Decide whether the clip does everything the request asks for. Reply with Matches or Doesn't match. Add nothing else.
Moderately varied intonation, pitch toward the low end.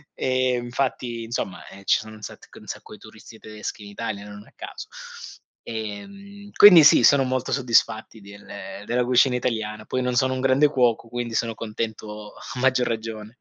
Matches